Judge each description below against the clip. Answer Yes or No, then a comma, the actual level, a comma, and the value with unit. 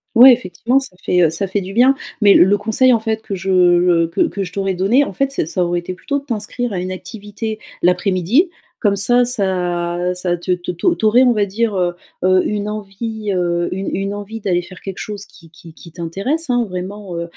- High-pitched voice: Yes, high, 195 Hz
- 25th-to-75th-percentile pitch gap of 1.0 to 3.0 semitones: No, average, 3.7 semitones